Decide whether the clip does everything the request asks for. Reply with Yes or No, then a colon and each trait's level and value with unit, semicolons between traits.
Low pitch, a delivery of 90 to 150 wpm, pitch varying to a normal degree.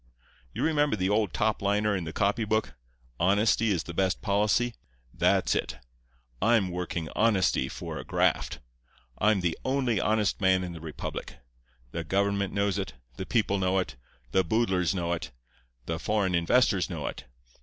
No: very low, 95 Hz; average, 160 wpm; average, 3.7 semitones